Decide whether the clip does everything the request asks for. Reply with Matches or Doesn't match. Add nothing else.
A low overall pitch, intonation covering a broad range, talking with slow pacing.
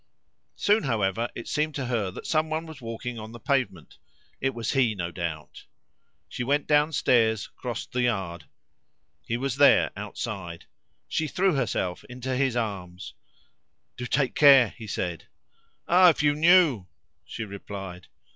Doesn't match